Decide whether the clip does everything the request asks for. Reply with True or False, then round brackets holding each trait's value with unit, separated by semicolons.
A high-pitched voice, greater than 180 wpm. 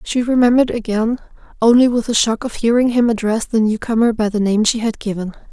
True (225 Hz; 205 wpm)